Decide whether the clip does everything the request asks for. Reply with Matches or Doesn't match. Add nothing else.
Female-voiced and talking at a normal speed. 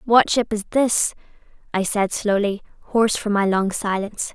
Matches